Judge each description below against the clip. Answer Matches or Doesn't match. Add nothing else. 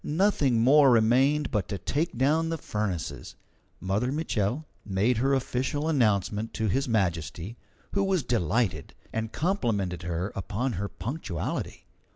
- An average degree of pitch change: Doesn't match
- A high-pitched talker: Doesn't match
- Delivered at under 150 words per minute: Matches